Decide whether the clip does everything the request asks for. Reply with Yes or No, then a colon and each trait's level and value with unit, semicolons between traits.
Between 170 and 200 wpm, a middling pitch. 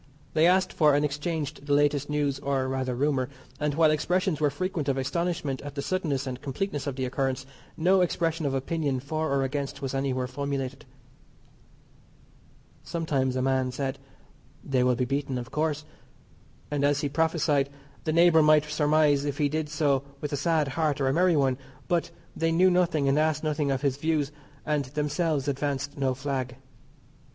Yes: average, 180 wpm; medium, 145 Hz